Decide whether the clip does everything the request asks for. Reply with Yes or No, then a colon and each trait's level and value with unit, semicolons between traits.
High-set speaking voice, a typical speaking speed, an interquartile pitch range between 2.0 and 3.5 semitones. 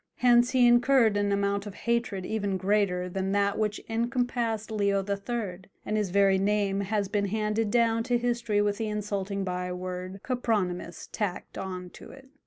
Yes: high, 205 Hz; average, 165 wpm; average, 2.8 semitones